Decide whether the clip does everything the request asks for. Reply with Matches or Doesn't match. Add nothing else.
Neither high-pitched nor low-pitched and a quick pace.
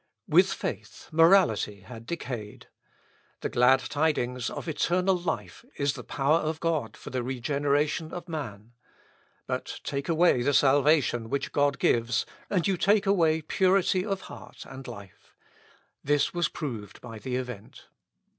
Doesn't match